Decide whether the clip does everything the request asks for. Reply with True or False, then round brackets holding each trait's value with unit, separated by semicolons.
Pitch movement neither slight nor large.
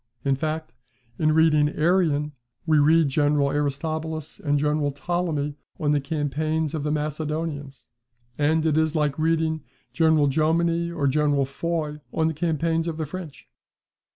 False (1.7 semitones)